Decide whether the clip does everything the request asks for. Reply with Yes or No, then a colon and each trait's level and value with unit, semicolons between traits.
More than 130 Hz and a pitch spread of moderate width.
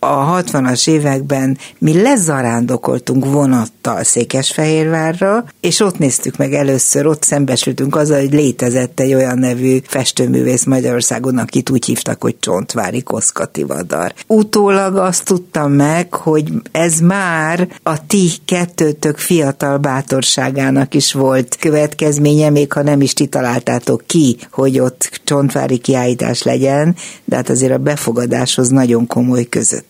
Yes: medium, 140 Hz; average, 3.4 semitones